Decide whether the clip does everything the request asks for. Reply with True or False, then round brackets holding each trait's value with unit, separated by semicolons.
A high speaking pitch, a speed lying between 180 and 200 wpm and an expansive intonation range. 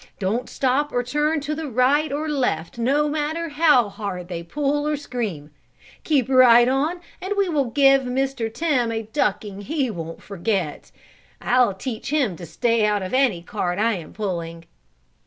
False (250 Hz; 165 wpm; 6.3 semitones)